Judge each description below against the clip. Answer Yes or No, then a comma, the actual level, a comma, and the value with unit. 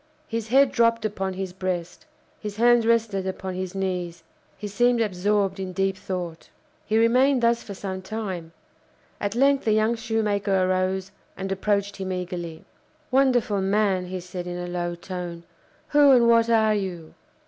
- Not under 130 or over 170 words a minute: Yes, average, 160 wpm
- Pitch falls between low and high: No, high, 195 Hz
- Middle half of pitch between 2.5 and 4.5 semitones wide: Yes, average, 3.5 semitones